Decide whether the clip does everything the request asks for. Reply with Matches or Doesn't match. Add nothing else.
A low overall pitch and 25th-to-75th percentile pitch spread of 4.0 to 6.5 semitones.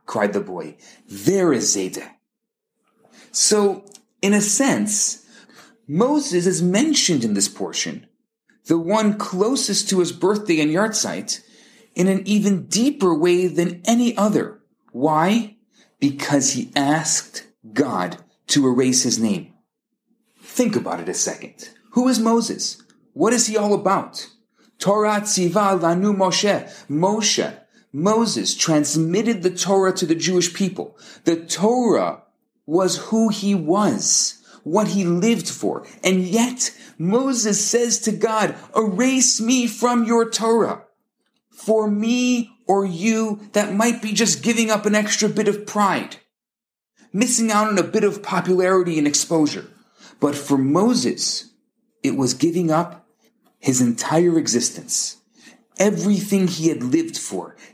Doesn't match